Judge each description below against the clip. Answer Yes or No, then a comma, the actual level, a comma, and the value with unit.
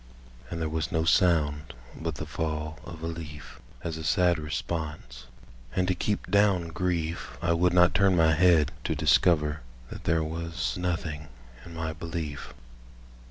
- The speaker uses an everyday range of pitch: No, narrow, 2.1 semitones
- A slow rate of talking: No, average, 160 wpm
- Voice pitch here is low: Yes, very low, 80 Hz